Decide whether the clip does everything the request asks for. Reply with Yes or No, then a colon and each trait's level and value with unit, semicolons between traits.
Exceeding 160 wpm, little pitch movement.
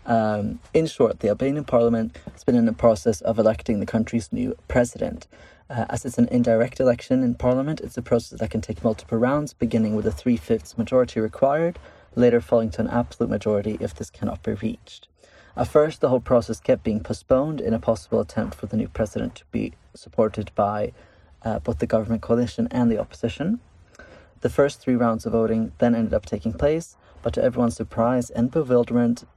Yes: average, 195 wpm; narrow, 1.9 semitones